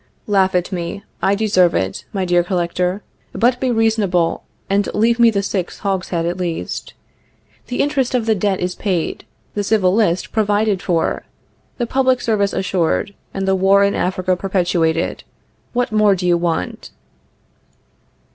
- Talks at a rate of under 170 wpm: Yes, average, 155 wpm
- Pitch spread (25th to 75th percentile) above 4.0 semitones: No, average, 3.3 semitones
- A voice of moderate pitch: No, high, 195 Hz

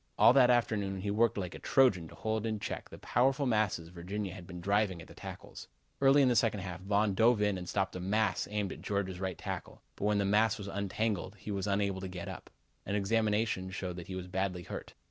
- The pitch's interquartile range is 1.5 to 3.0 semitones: Yes, average, 2.7 semitones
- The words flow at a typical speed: No, fast, 235 wpm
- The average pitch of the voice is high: No, low, 100 Hz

